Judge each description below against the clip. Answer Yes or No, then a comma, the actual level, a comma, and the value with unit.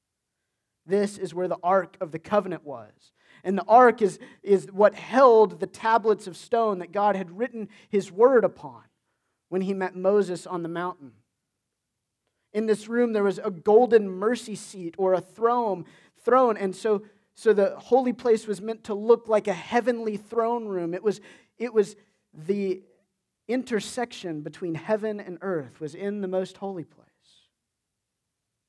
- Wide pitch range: No, average, 3.3 semitones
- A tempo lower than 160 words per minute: No, average, 165 wpm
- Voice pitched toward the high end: Yes, high, 200 Hz